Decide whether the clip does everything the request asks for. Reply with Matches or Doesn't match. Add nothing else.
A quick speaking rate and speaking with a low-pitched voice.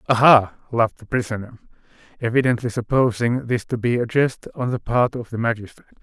Doesn't match